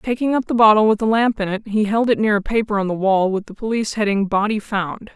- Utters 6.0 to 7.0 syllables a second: Yes, 6.1 syllables/s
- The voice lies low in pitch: No, high, 210 Hz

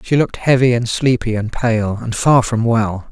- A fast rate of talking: Yes, fast, 210 wpm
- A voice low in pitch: Yes, low, 115 Hz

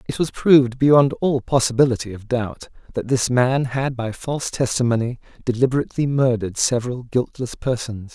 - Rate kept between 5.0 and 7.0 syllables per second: Yes, 5.4 syllables/s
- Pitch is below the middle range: Yes, low, 125 Hz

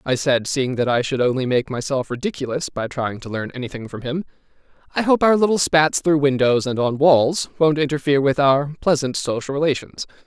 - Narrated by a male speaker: Yes, male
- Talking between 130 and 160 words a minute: No, average, 200 wpm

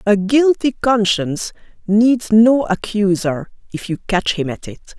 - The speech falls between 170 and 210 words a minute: No, average, 145 wpm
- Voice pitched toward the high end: Yes, high, 210 Hz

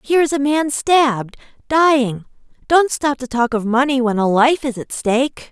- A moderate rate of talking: Yes, average, 195 wpm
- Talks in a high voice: Yes, very high, 265 Hz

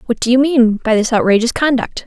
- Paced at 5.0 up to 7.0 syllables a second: Yes, 5.8 syllables/s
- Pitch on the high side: Yes, high, 240 Hz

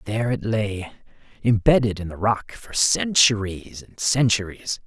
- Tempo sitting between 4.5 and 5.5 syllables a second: No, 4.3 syllables/s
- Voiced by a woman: No, male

